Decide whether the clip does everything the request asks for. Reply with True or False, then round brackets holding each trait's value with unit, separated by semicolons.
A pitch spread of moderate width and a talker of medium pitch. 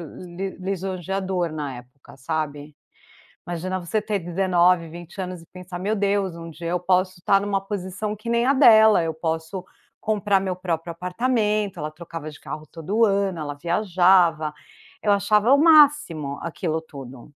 True (3.5 semitones; 180 Hz)